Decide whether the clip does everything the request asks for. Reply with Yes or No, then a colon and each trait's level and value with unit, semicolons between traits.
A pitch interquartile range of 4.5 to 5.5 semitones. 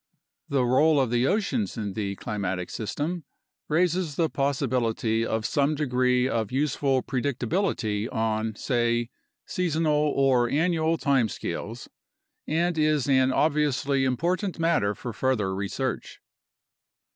Yes: average, 4.9 semitones